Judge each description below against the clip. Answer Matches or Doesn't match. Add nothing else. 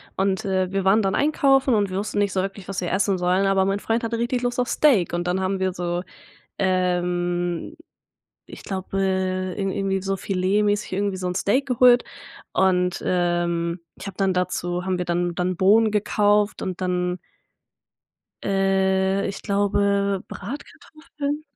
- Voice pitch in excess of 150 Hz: Matches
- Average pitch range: Doesn't match